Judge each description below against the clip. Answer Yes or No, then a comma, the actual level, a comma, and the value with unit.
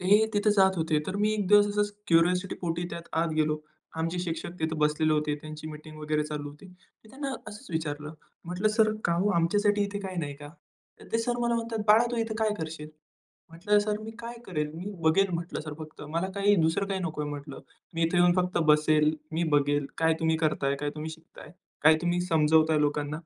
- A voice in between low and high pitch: Yes, medium, 165 Hz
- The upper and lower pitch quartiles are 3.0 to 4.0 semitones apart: No, average, 4.9 semitones